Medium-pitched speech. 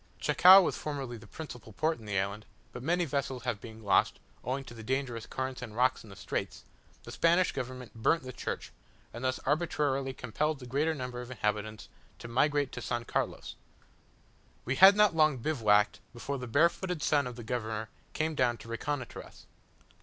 No: low, 130 Hz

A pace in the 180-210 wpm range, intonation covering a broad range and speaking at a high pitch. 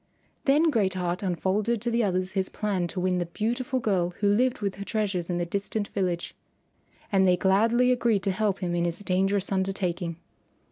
No: average, 190 wpm; average, 3.0 semitones; high, 195 Hz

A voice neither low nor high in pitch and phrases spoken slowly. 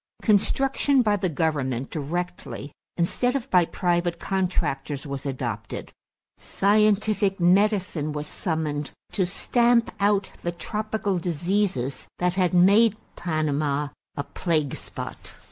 Yes: medium, 175 Hz; slow, 110 wpm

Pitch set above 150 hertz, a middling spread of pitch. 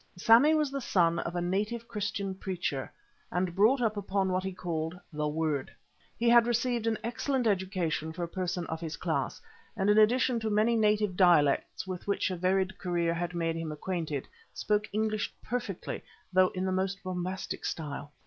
Yes: high, 190 Hz; average, 3.9 semitones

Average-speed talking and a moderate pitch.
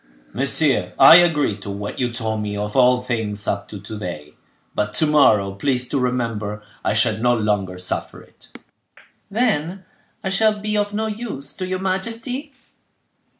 No: average, 165 wpm; low, 125 Hz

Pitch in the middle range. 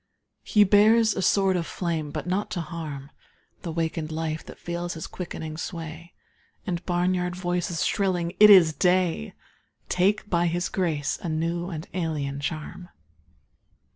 Yes: medium, 175 Hz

